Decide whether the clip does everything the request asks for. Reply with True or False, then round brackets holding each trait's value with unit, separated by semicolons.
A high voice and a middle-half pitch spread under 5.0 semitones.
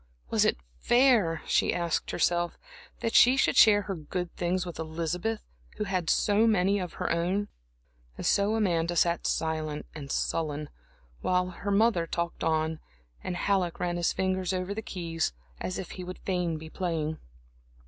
False (180 Hz; 3.2 semitones)